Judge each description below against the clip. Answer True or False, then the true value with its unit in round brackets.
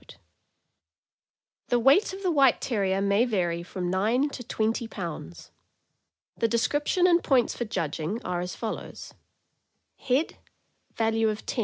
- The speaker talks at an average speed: False (125 wpm)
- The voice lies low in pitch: False (225 Hz)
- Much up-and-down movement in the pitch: True (5.7 semitones)